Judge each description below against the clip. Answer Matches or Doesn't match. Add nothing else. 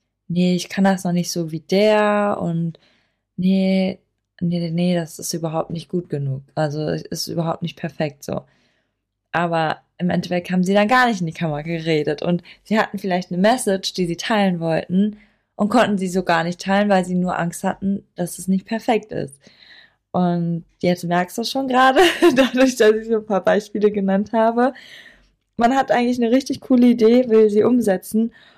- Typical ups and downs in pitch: Matches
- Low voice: Doesn't match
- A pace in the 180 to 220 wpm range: Matches